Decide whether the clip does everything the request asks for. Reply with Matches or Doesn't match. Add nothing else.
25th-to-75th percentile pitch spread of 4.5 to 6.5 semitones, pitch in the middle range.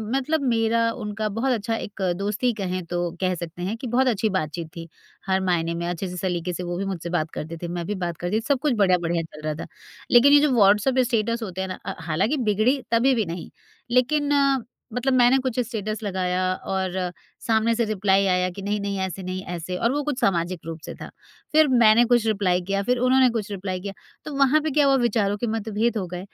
Doesn't match